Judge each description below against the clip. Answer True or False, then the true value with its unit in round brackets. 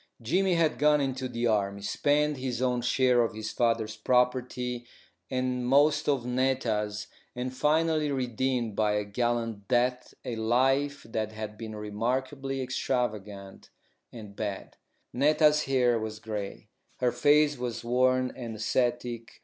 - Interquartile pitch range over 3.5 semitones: False (3.1 semitones)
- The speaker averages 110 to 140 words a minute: True (135 wpm)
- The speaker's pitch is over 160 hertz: False (125 Hz)